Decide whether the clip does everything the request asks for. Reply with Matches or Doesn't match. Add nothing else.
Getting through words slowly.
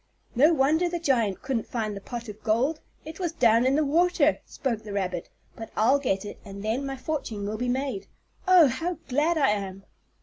Doesn't match